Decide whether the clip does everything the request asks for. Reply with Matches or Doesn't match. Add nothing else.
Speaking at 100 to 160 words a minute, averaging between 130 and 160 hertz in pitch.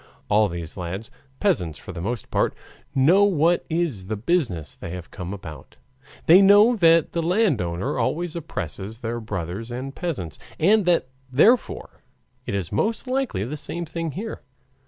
Matches